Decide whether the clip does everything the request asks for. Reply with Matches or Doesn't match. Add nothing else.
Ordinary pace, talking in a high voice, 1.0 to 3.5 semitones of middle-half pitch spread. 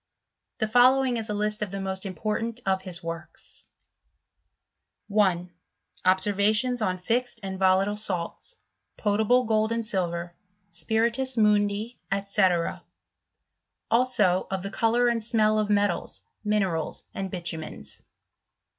Doesn't match